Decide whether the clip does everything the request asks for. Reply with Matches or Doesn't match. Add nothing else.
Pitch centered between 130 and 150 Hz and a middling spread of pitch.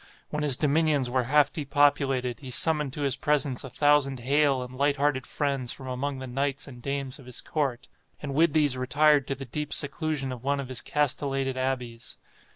Doesn't match